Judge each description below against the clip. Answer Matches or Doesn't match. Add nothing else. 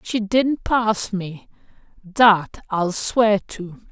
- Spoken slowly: Matches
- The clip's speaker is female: Matches